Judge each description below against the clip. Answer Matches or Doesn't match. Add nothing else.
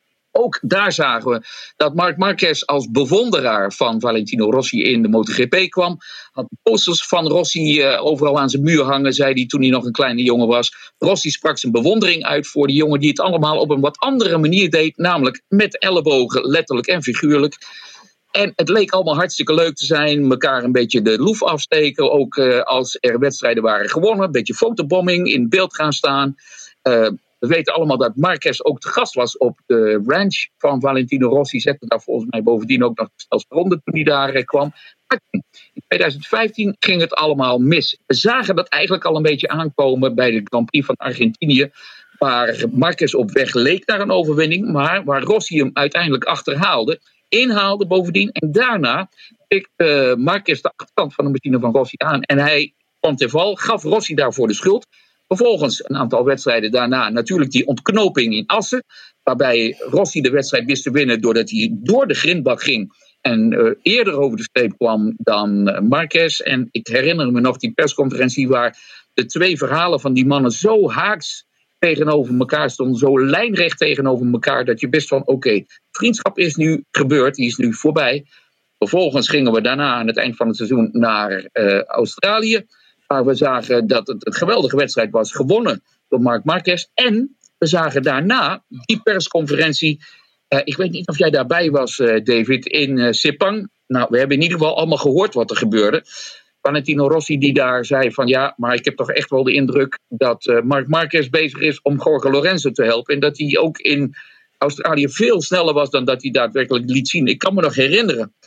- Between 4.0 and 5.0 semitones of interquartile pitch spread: Doesn't match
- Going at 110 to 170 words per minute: Doesn't match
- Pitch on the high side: Doesn't match